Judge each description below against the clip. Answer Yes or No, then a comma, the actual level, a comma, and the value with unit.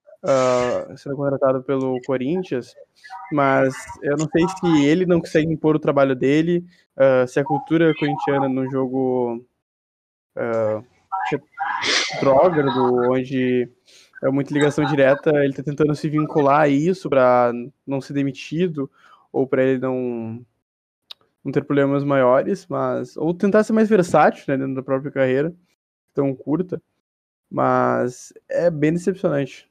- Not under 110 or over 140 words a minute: Yes, average, 135 wpm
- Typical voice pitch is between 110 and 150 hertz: Yes, medium, 140 Hz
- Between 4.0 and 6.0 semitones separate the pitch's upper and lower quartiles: No, average, 3.3 semitones